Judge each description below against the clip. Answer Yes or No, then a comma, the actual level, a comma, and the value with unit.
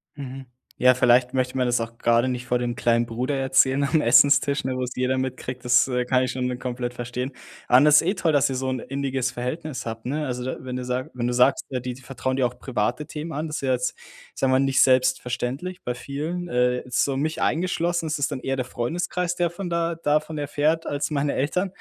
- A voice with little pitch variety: No, average, 3.1 semitones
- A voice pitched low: Yes, low, 130 Hz